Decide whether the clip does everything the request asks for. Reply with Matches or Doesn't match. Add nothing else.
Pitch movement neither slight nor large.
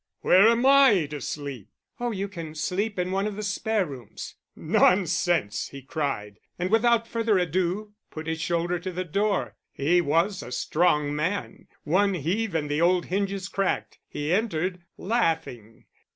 Matches